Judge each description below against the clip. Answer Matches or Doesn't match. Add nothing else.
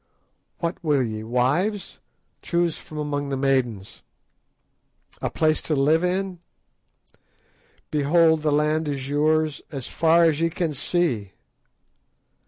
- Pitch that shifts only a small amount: Doesn't match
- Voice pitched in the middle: Matches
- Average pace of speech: Doesn't match